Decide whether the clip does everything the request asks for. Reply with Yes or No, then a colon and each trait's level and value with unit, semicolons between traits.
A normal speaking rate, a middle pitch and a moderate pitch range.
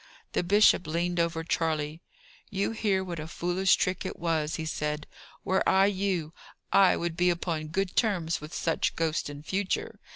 Yes: average, 170 wpm; medium, 170 Hz; average, 3.0 semitones